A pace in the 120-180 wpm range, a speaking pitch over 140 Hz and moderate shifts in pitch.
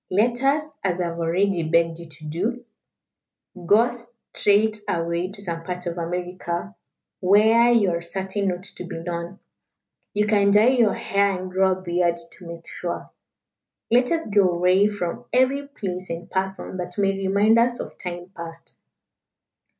Yes: average, 165 wpm; medium, 185 Hz; average, 3.4 semitones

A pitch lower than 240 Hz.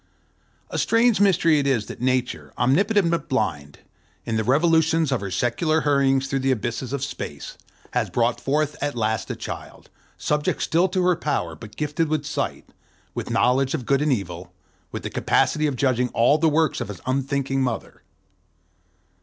Yes: low, 135 Hz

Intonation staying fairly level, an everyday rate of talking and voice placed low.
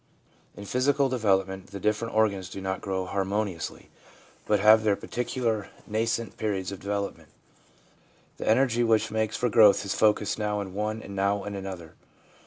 Yes: narrow, 2.2 semitones; average, 160 wpm; low, 105 Hz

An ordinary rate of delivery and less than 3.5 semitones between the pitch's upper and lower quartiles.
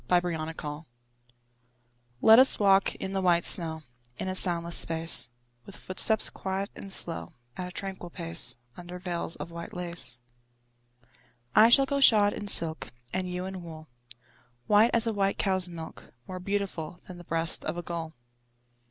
Yes: average, 160 wpm; average, 2.8 semitones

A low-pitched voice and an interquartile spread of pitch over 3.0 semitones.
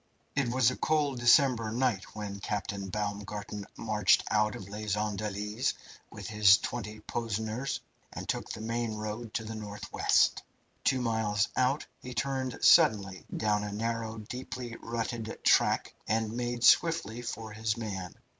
No: low, 110 Hz; narrow, 2.4 semitones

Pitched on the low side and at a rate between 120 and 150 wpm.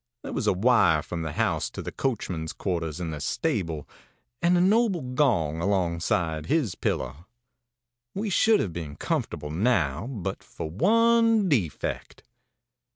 Yes: very low, 95 Hz; average, 145 wpm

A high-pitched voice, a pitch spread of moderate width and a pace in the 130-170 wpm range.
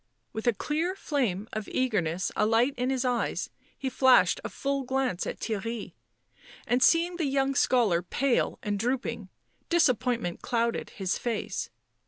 Yes: high, 245 Hz; average, 3.8 semitones; average, 150 wpm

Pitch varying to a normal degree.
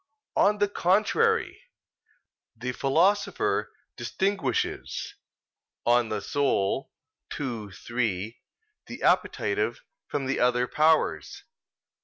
No: wide, 8.8 semitones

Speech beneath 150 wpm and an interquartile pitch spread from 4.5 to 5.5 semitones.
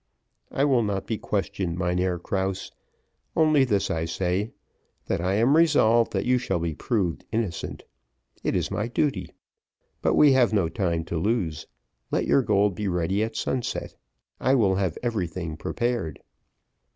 No: average, 155 wpm; average, 5.0 semitones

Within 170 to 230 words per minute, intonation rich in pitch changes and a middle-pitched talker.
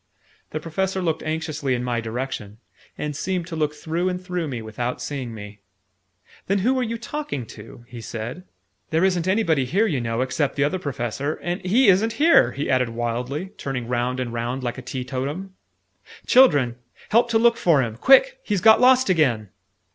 Yes: average, 185 wpm; wide, 7.4 semitones; medium, 150 Hz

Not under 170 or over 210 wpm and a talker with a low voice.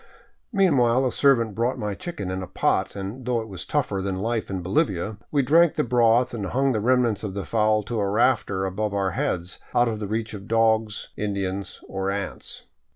Yes: average, 200 wpm; low, 110 Hz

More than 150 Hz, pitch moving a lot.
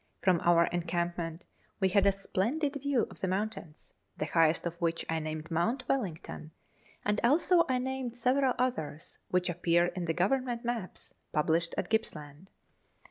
Yes: medium, 185 Hz; wide, 6.6 semitones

